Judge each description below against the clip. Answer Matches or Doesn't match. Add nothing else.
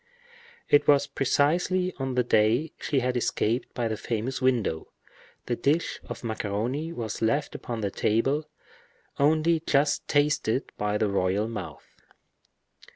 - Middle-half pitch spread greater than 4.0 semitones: Matches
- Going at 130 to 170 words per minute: Matches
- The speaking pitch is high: Doesn't match